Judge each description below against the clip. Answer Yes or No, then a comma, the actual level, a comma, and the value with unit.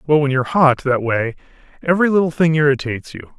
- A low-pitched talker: No, medium, 145 Hz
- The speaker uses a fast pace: Yes, fast, 215 wpm